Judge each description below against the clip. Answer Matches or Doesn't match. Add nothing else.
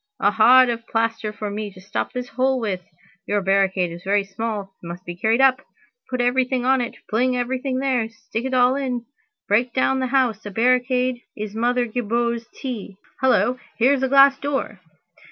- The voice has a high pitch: Matches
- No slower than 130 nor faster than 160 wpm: Doesn't match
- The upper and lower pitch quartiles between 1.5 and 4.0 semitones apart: Matches